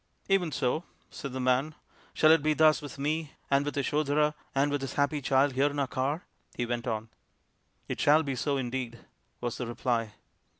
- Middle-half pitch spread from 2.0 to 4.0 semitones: Yes, average, 2.8 semitones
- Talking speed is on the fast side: Yes, fast, 215 wpm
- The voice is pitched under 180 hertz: Yes, medium, 140 Hz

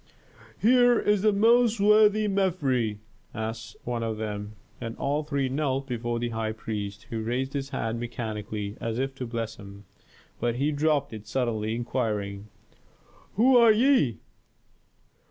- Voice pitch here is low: Yes, low, 120 Hz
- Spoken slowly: No, average, 145 wpm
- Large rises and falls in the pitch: Yes, wide, 6.1 semitones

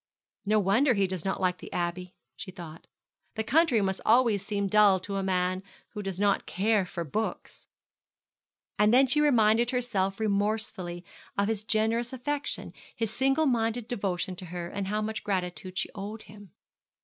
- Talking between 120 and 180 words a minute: Yes, average, 170 wpm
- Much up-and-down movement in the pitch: No, average, 3.2 semitones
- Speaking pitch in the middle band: No, high, 205 Hz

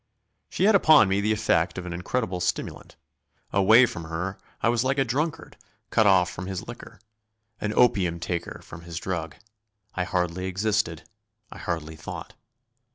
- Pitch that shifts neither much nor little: Yes, average, 4.4 semitones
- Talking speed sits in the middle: Yes, average, 160 wpm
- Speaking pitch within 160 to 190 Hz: No, very low, 95 Hz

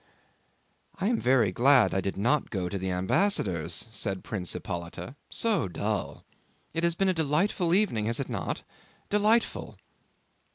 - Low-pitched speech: Yes, low, 120 Hz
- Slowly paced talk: No, average, 150 wpm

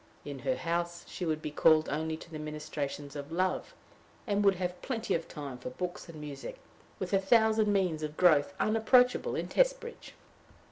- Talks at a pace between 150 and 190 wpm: Yes, average, 180 wpm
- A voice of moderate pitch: Yes, medium, 170 Hz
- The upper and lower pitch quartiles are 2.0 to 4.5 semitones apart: No, average, 5.2 semitones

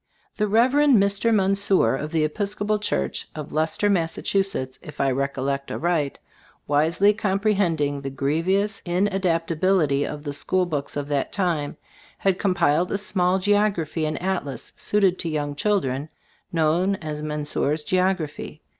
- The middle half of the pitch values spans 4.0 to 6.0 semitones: Yes, average, 4.9 semitones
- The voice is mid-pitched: Yes, medium, 170 Hz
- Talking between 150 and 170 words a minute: No, slow, 135 wpm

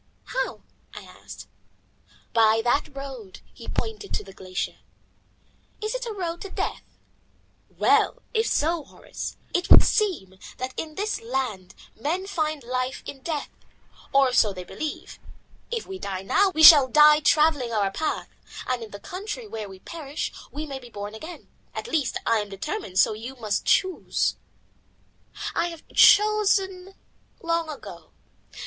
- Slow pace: No, average, 155 wpm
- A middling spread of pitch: No, wide, 8.2 semitones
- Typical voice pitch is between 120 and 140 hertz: No, very high, 295 Hz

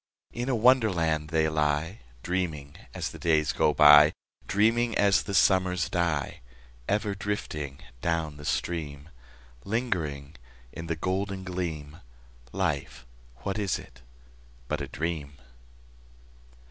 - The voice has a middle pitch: No, very low, 85 Hz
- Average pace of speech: No, slow, 120 wpm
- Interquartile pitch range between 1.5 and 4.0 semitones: No, average, 4.6 semitones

